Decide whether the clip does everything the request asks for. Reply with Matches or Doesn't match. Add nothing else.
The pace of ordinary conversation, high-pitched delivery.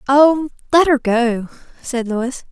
Matches